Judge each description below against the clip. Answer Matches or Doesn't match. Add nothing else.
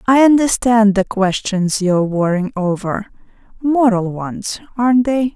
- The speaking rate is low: Matches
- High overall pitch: Matches